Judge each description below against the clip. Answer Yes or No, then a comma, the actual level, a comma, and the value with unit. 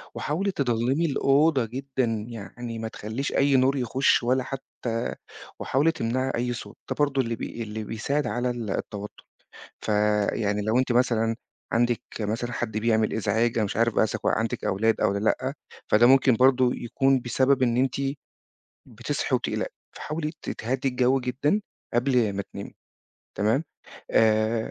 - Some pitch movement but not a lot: Yes, average, 3.1 semitones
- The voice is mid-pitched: No, low, 120 Hz